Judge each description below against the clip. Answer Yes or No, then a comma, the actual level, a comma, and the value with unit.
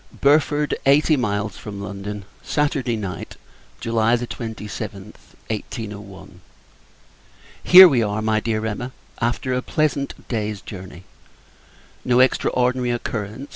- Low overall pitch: Yes, low, 115 Hz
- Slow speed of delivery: Yes, slow, 105 wpm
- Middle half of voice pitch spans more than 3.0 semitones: Yes, average, 3.6 semitones